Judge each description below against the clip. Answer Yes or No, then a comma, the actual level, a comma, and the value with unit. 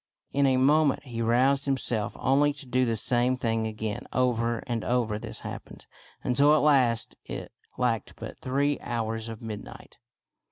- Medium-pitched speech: No, low, 125 Hz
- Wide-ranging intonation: No, average, 3.1 semitones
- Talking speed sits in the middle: Yes, average, 160 wpm